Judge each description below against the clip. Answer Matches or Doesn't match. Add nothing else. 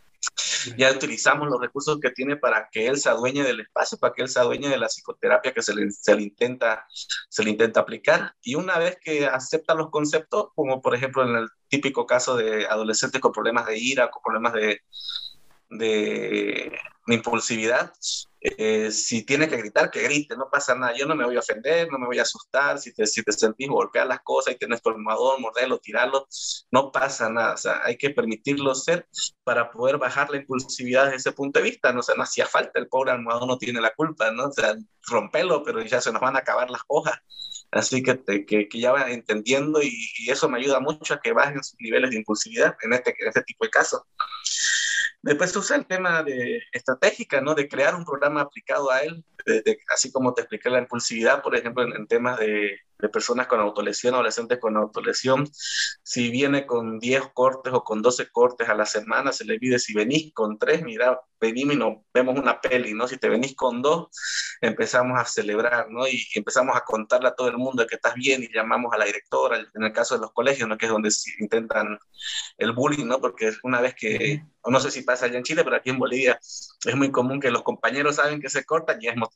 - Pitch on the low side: Matches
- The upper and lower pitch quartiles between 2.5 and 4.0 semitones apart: Doesn't match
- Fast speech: Matches